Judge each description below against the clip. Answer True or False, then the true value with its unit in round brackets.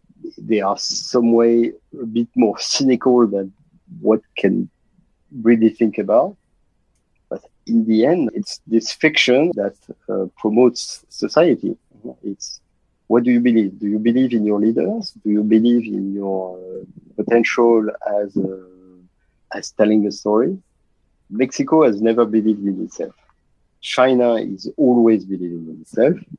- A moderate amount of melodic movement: True (3.4 semitones)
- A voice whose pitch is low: True (110 Hz)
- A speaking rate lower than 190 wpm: True (140 wpm)